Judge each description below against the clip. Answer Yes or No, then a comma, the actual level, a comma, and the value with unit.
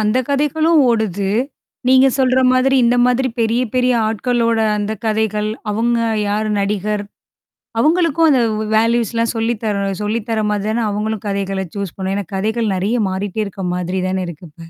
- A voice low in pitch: No, high, 220 Hz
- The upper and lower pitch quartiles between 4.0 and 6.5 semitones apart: No, average, 3.3 semitones